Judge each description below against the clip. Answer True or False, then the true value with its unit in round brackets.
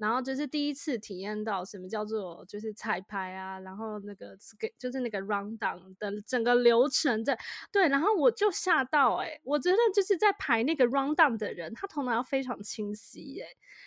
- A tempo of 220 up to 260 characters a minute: False (365 characters per minute)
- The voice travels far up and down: True (5.7 semitones)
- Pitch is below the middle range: False (235 Hz)